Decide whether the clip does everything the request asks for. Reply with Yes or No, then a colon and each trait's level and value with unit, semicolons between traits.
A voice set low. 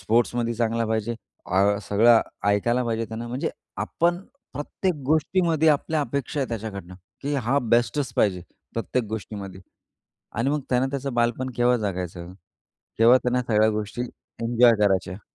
Yes: low, 120 Hz